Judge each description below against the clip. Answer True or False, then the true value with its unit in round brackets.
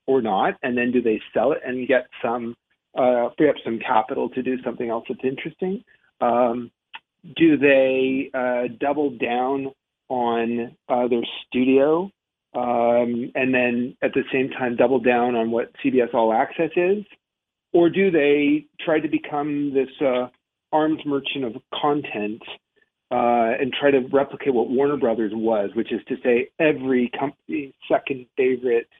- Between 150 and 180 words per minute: True (155 wpm)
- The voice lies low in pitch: True (130 Hz)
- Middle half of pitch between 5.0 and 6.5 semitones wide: False (3.1 semitones)